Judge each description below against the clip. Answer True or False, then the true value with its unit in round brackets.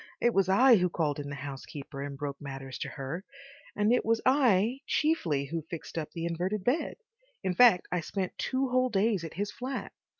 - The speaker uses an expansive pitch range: True (7.9 semitones)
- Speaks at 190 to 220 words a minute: True (200 wpm)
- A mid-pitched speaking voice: True (180 Hz)